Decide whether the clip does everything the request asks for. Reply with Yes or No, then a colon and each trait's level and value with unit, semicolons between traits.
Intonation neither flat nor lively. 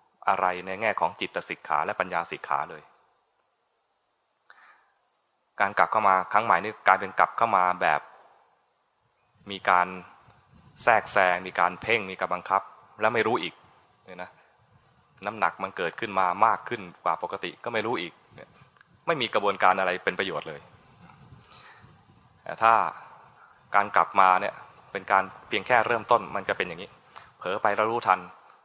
No: narrow, 1.8 semitones